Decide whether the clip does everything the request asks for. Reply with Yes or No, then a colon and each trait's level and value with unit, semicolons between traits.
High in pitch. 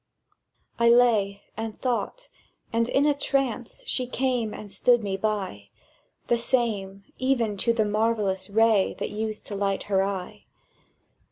Yes: high, 220 Hz